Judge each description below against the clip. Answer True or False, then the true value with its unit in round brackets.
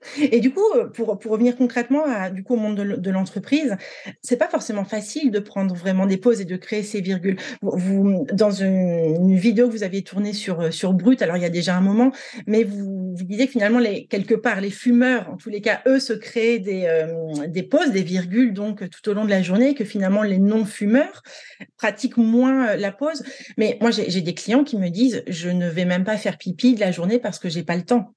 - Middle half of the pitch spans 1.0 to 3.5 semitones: False (4.3 semitones)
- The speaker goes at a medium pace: False (245 wpm)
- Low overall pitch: False (210 Hz)